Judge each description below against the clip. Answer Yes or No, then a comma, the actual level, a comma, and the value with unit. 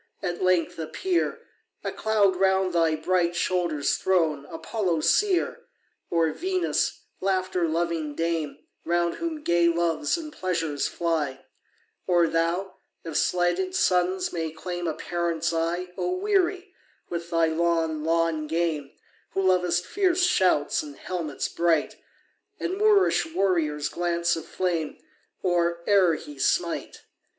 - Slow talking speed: Yes, slow, 125 wpm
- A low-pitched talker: No, medium, 175 Hz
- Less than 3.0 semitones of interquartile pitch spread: Yes, narrow, 2.4 semitones